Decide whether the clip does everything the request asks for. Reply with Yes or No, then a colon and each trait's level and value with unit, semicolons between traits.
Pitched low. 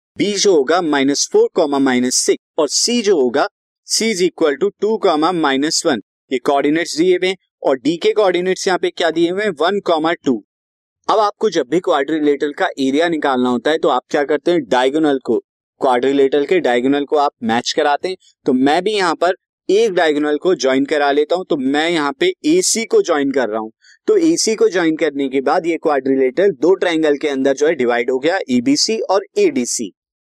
No: medium, 165 Hz